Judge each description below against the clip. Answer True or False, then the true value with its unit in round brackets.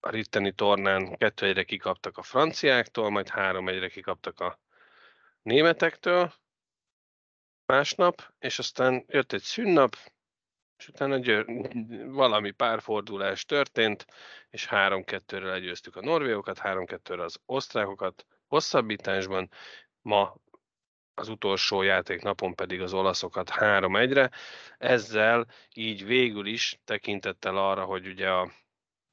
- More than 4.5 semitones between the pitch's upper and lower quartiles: True (4.9 semitones)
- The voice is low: True (100 Hz)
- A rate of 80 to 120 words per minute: True (105 wpm)